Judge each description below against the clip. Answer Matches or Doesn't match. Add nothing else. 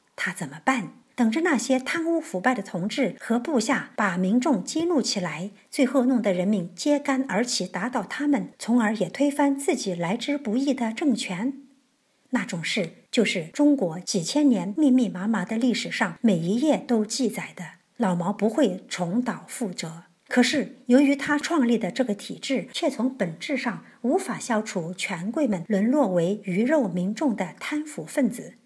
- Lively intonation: Matches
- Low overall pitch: Doesn't match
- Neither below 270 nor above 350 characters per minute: Doesn't match